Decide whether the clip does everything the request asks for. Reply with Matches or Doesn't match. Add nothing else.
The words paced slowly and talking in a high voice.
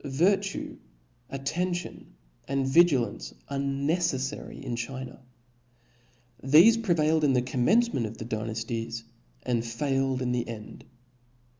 Doesn't match